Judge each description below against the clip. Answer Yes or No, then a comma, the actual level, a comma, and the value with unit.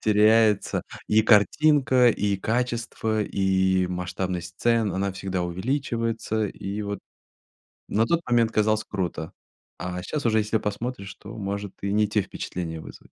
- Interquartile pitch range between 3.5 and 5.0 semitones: No, average, 3.0 semitones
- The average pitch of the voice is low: Yes, low, 105 Hz